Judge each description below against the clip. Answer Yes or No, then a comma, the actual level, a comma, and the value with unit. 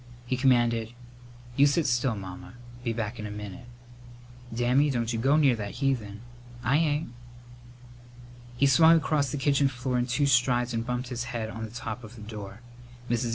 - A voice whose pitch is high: No, low, 120 Hz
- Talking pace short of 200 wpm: Yes, average, 180 wpm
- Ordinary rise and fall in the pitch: Yes, average, 3.1 semitones